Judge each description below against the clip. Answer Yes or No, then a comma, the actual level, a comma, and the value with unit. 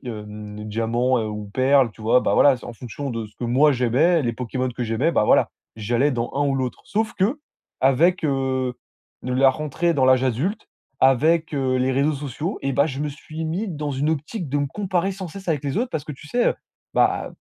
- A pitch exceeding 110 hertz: Yes, low, 135 Hz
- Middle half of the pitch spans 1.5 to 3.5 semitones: No, average, 4.1 semitones